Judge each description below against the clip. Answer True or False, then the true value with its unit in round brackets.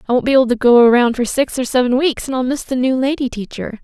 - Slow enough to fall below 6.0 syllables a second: False (6.6 syllables/s)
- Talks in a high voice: True (250 Hz)